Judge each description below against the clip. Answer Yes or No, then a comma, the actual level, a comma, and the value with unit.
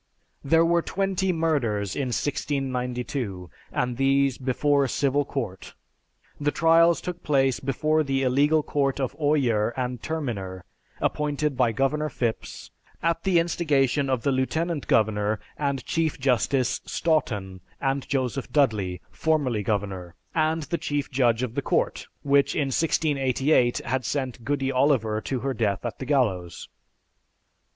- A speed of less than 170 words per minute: Yes, average, 140 wpm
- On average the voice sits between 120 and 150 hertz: Yes, low, 135 Hz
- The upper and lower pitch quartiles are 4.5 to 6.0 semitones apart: No, average, 3.7 semitones